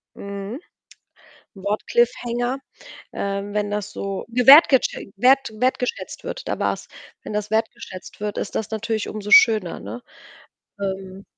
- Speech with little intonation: No, average, 3.2 semitones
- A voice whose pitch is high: Yes, high, 210 Hz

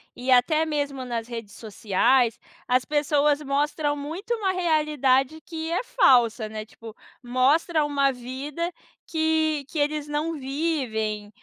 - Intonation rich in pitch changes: No, average, 4.0 semitones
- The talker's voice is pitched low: No, very high, 285 Hz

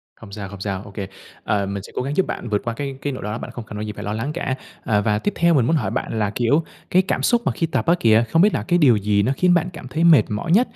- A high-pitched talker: No, low, 120 Hz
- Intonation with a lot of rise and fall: Yes, wide, 7.8 semitones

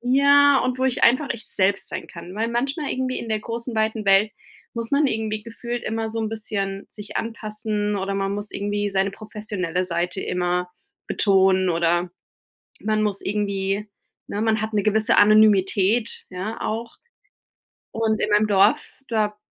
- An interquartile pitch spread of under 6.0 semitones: Yes, narrow, 2.5 semitones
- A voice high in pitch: Yes, high, 215 Hz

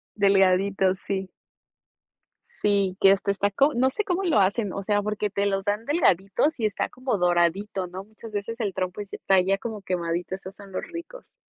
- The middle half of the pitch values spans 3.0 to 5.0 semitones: No, narrow, 2.4 semitones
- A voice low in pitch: No, high, 200 Hz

